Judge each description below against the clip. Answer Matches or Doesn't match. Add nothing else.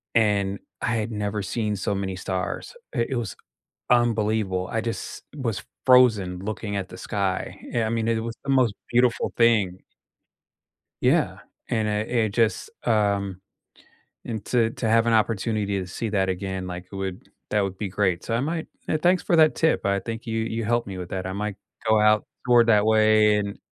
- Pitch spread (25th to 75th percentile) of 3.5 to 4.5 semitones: Doesn't match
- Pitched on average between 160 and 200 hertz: Doesn't match